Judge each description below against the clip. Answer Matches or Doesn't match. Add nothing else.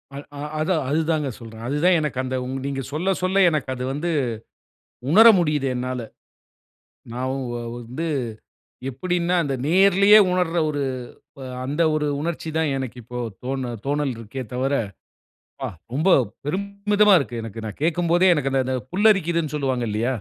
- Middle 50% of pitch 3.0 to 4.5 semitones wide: Doesn't match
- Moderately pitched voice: Matches